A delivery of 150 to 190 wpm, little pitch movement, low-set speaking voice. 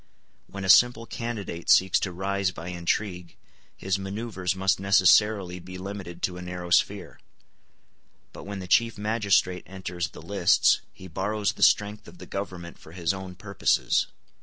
Yes: average, 160 wpm; narrow, 2.2 semitones; very low, 95 Hz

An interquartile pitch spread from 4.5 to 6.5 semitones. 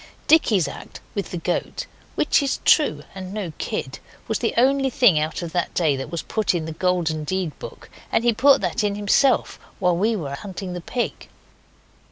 Yes: wide, 5.5 semitones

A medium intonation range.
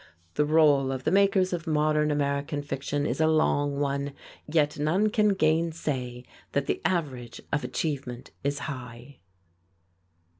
No: narrow, 2.2 semitones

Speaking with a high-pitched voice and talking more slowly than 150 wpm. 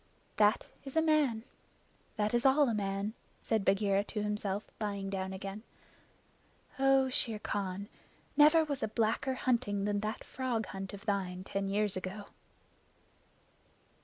Yes: high, 210 Hz; average, 140 wpm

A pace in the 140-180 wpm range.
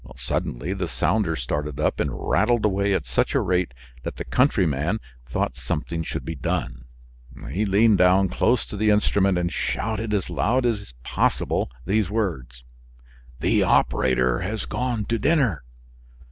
Yes: average, 150 wpm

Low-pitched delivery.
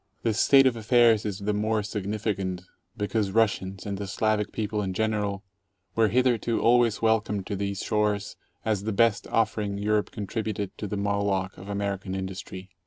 Yes: low, 105 Hz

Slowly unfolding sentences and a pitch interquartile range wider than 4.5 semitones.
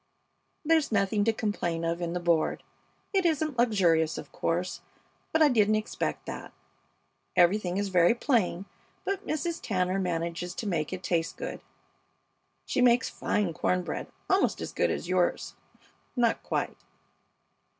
No: average, 145 wpm; wide, 5.5 semitones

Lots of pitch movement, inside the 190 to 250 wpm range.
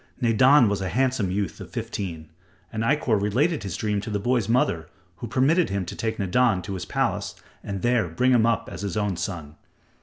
No: average, 4.4 semitones; fast, 205 wpm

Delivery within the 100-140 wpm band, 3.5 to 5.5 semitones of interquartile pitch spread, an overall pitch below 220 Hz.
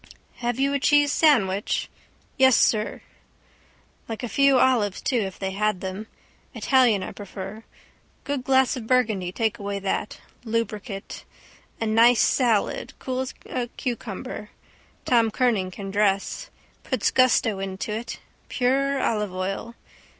No: slow, 135 wpm; average, 4.2 semitones; high, 225 Hz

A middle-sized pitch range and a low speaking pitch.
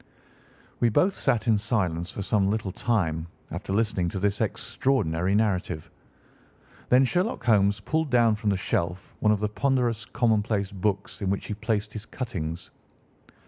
Yes: average, 3.2 semitones; low, 105 Hz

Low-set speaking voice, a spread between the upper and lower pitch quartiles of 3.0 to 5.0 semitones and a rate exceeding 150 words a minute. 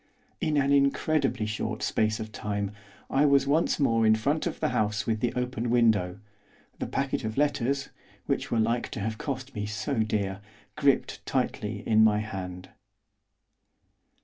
Yes: low, 115 Hz; average, 4.4 semitones; average, 160 wpm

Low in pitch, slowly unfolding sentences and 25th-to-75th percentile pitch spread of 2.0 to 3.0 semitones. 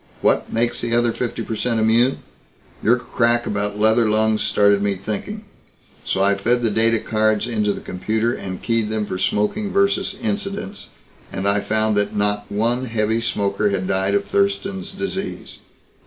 No: low, 110 Hz; average, 170 wpm; narrow, 2.6 semitones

